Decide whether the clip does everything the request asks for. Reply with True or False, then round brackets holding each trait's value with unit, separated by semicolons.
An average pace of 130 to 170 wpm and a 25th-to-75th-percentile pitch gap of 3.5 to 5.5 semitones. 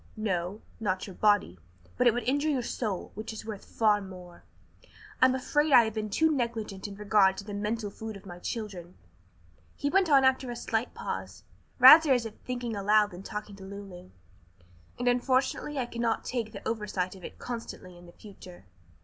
False (190 wpm; 3.9 semitones)